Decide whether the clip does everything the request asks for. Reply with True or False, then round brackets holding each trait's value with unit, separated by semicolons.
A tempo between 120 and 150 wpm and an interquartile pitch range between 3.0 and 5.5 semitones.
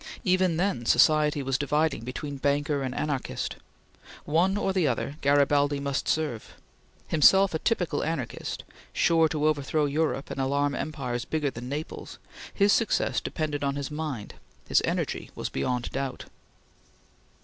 False (140 wpm; 2.5 semitones)